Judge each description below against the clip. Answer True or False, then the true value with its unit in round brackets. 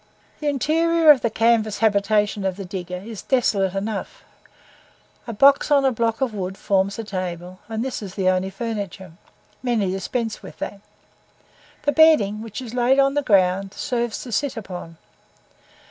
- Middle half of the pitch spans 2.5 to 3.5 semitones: False (4.5 semitones)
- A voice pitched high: True (215 Hz)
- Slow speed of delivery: False (165 wpm)